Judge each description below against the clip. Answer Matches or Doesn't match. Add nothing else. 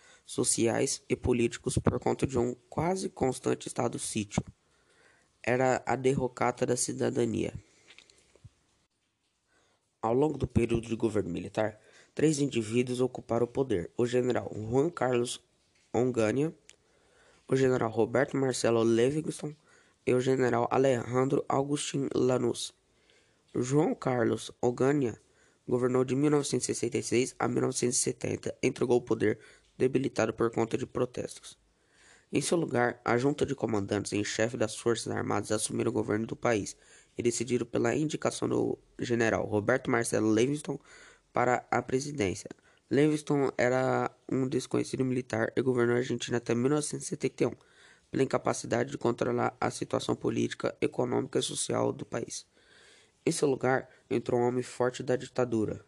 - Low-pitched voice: Matches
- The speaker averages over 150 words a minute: Doesn't match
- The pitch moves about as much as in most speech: Doesn't match